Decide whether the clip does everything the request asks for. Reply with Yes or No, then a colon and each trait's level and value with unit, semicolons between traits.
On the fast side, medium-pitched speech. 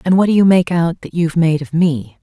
Yes: fast, 295 wpm; medium, 165 Hz